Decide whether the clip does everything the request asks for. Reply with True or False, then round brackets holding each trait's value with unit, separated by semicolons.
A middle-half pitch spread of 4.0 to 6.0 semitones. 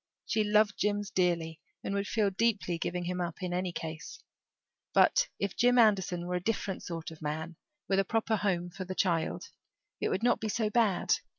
False (3.3 semitones)